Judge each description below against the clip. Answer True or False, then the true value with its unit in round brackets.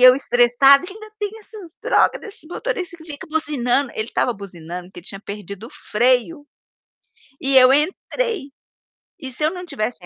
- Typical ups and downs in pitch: False (6.8 semitones)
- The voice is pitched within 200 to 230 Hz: False (270 Hz)